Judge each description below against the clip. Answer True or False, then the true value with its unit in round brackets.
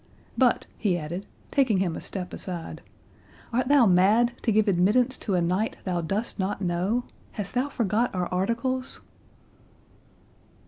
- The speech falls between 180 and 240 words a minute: False (145 wpm)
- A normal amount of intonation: True (4.8 semitones)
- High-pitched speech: True (205 Hz)